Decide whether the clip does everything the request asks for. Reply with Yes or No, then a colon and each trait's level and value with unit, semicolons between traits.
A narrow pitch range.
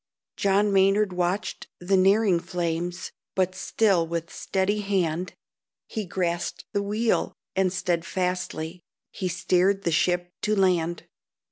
Yes: narrow, 2.2 semitones